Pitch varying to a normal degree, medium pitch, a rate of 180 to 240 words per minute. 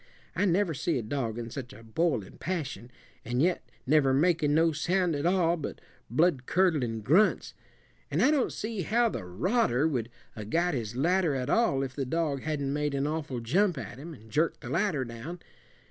No: wide, 5.7 semitones; medium, 150 Hz; average, 190 wpm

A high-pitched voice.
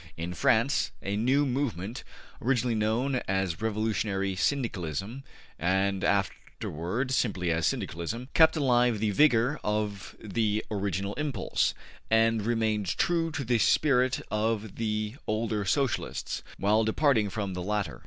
No: low, 110 Hz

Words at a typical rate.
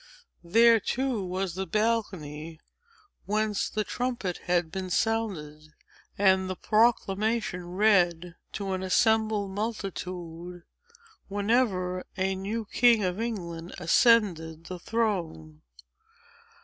No: slow, 100 wpm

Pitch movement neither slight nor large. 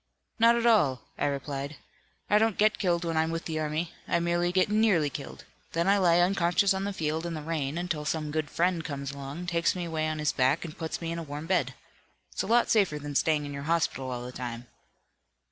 Yes: average, 3.3 semitones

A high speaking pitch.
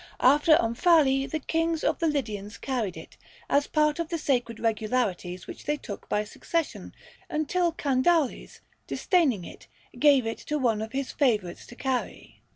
Yes: very high, 270 Hz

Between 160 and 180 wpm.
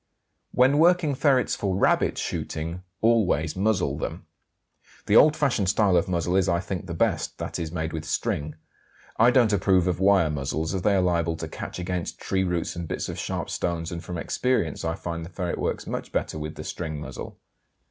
No: average, 200 wpm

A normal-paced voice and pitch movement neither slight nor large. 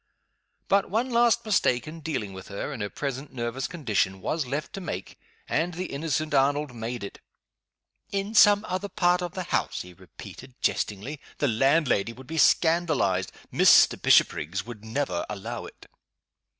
No: average, 160 wpm; wide, 7.9 semitones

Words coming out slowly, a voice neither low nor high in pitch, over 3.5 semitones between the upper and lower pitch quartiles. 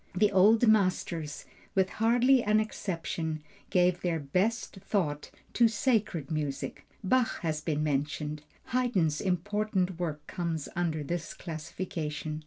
Yes: slow, 120 wpm; medium, 175 Hz; average, 5.2 semitones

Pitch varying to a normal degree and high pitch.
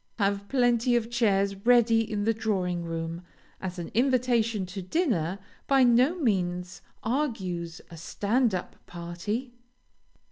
Yes: average, 5.0 semitones; high, 210 Hz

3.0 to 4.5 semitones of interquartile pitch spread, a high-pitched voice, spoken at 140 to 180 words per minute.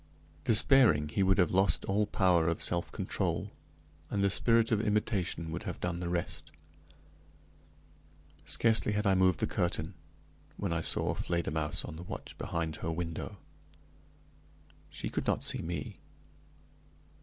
No: average, 3.5 semitones; very low, 90 Hz; average, 145 wpm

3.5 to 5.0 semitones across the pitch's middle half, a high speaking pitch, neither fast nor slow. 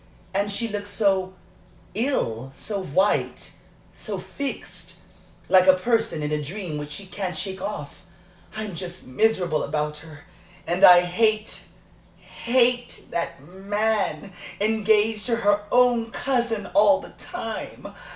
No: average, 4.1 semitones; high, 200 Hz; slow, 130 wpm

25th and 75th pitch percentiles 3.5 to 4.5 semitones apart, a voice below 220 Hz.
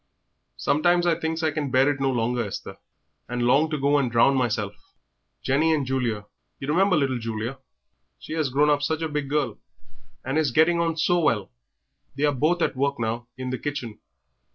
Yes: average, 4.2 semitones; medium, 140 Hz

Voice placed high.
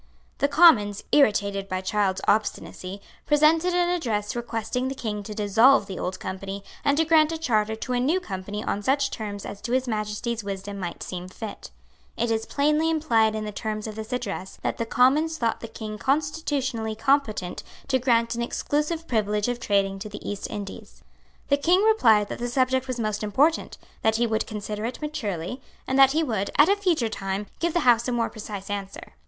Yes: high, 225 Hz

